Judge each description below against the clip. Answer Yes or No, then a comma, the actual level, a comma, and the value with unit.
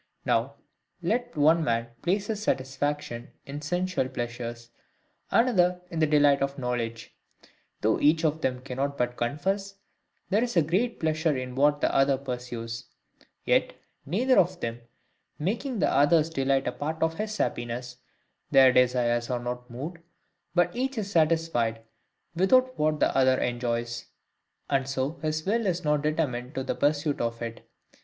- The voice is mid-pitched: Yes, medium, 145 Hz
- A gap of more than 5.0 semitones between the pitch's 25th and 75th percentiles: Yes, wide, 5.4 semitones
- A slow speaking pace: No, average, 150 wpm